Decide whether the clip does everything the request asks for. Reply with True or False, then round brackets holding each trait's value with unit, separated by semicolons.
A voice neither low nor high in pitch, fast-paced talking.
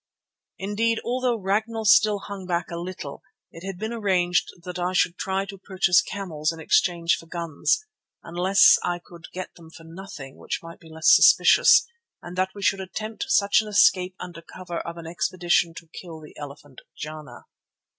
False (180 Hz; 175 wpm)